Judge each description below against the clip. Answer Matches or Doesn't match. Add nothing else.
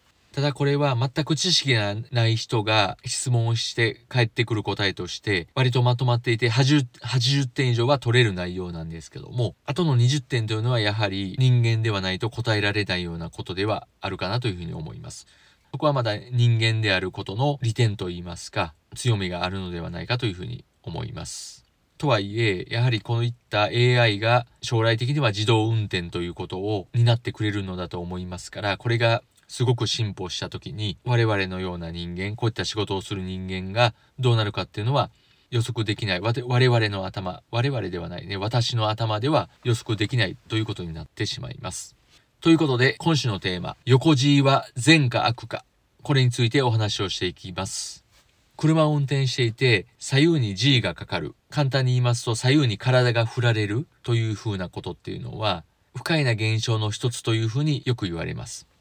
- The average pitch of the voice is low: Matches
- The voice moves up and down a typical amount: Matches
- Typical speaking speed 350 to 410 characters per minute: Matches